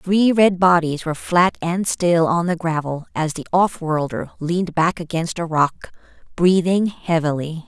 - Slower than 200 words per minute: Yes, average, 165 wpm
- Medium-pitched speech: Yes, medium, 170 Hz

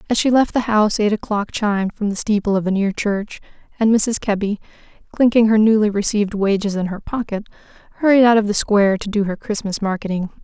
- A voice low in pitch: No, high, 210 Hz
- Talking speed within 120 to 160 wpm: No, fast, 205 wpm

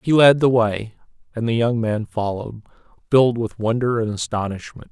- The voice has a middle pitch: No, low, 115 Hz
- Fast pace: No, average, 170 wpm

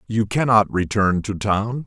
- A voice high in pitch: No, low, 105 Hz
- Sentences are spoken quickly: No, average, 160 wpm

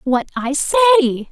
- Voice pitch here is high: Yes, very high, 310 Hz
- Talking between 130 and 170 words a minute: Yes, slow, 135 wpm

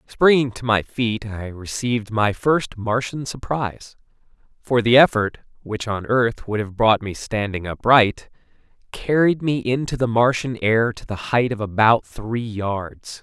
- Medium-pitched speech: No, low, 115 Hz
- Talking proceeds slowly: No, average, 160 wpm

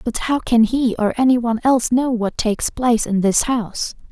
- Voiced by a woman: Yes, female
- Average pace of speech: No, fast, 220 wpm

